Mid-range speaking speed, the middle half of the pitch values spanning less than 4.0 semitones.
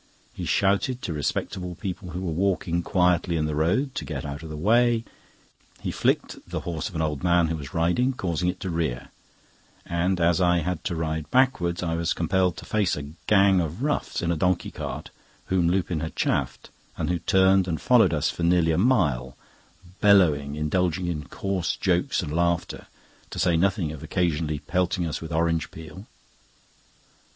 Yes: average, 185 wpm; average, 2.7 semitones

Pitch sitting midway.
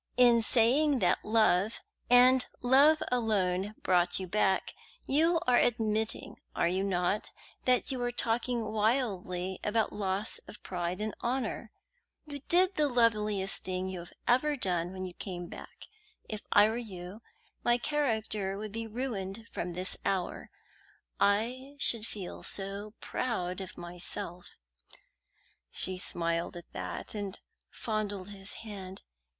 No: high, 210 Hz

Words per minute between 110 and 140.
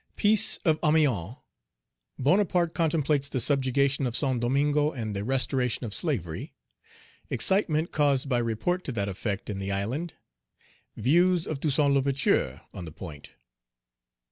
Yes: slow, 135 wpm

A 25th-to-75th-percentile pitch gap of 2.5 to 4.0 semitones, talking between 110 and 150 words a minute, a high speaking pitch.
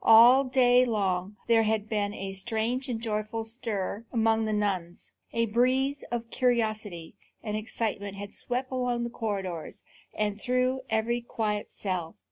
Yes: average, 2.8 semitones; average, 145 wpm; high, 220 Hz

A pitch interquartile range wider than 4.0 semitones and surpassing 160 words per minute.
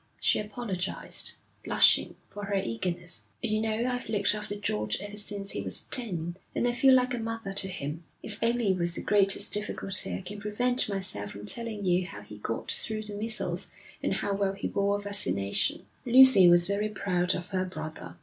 No: average, 3.5 semitones; average, 190 wpm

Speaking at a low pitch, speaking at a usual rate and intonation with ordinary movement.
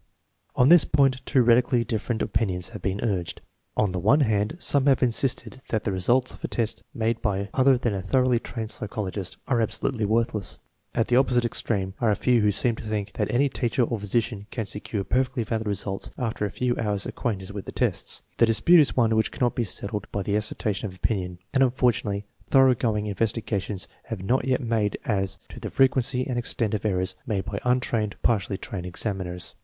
No: low, 110 Hz; fast, 210 wpm; average, 3.5 semitones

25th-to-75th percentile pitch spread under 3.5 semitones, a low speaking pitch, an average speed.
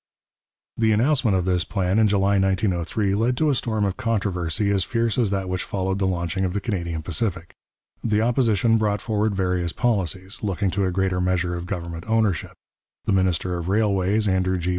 Yes: average, 3.0 semitones; very low, 95 Hz; average, 185 wpm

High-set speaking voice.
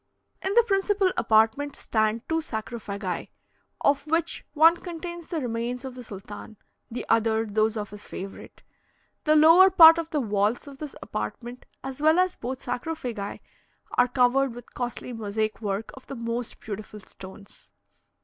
Yes: high, 245 Hz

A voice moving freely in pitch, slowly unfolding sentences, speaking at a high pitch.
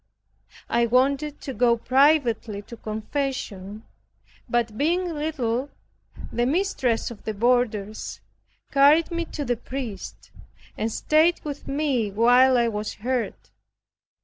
No: average, 4.3 semitones; slow, 120 wpm; high, 245 Hz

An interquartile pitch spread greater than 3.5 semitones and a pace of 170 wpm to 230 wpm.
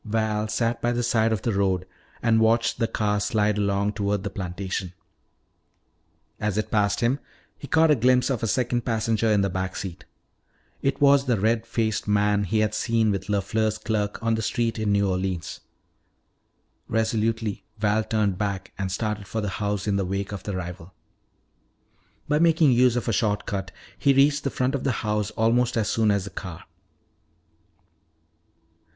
No: narrow, 2.5 semitones; average, 180 wpm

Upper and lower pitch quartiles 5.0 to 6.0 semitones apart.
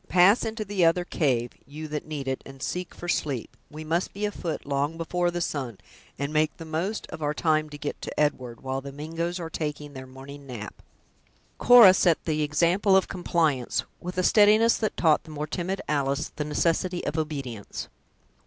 No: average, 3.8 semitones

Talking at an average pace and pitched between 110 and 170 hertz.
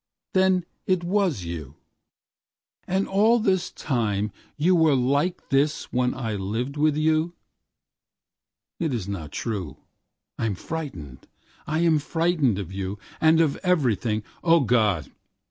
No: slow, 110 wpm; medium, 140 Hz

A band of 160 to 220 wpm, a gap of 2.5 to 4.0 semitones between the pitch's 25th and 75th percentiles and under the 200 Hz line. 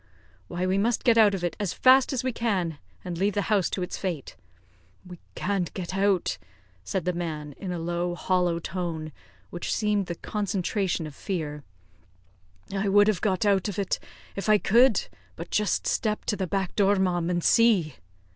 Yes: average, 185 wpm; average, 2.9 semitones; high, 190 Hz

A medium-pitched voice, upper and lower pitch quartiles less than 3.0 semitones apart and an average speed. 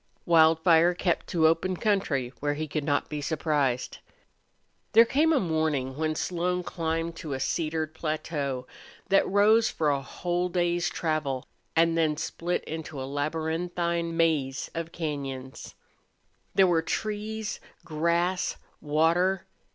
No: medium, 160 Hz; narrow, 2.6 semitones; slow, 130 wpm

